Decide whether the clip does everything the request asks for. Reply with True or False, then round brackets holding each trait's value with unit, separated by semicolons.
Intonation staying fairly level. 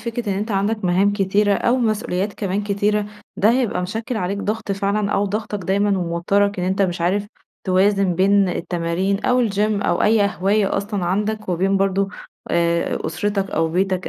True (2.0 semitones)